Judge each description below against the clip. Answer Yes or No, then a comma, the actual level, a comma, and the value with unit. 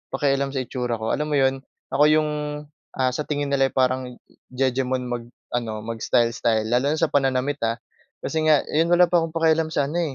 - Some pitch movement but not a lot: Yes, average, 3.5 semitones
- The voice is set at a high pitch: No, low, 135 Hz